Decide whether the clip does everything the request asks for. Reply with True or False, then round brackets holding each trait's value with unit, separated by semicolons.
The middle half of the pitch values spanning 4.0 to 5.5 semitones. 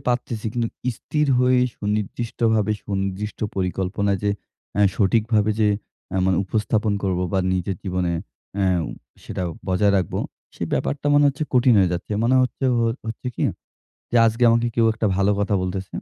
False (3.3 semitones)